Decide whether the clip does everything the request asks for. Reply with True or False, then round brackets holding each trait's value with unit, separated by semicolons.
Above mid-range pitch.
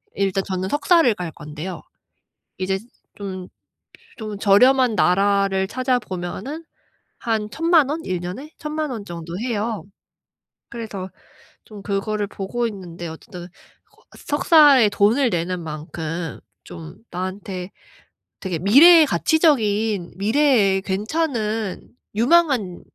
True (205 Hz)